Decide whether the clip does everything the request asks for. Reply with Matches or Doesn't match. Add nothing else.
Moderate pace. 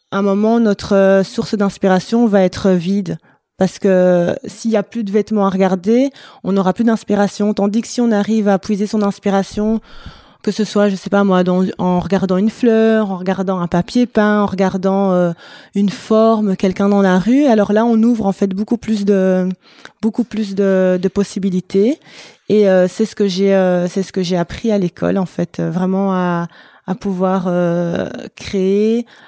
Matches